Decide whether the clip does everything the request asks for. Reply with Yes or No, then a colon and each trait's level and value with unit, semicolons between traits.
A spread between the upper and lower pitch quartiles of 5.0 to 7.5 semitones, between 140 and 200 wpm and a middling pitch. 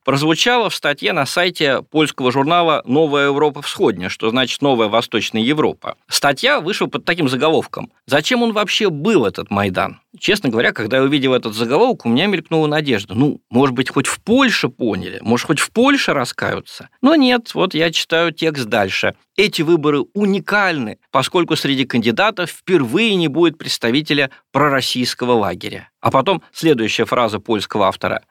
Yes: wide, 5.4 semitones; average, 155 wpm; medium, 145 Hz